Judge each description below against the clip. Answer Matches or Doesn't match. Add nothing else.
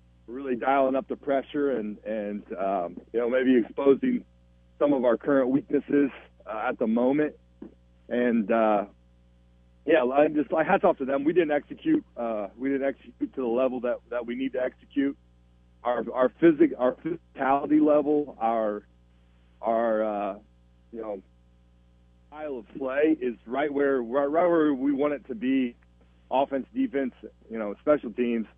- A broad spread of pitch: Matches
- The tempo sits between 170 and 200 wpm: Doesn't match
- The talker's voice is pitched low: Matches